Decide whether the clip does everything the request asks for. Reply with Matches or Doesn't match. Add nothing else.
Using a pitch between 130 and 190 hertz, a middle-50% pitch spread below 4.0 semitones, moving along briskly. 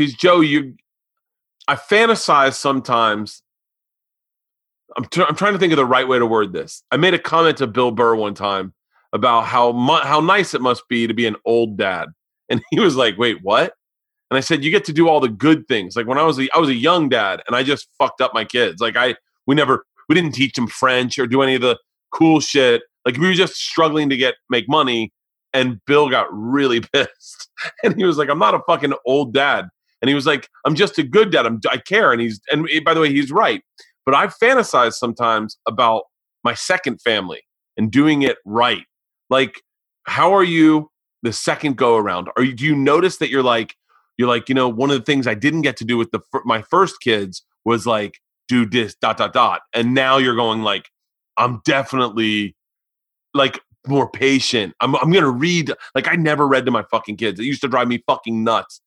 Doesn't match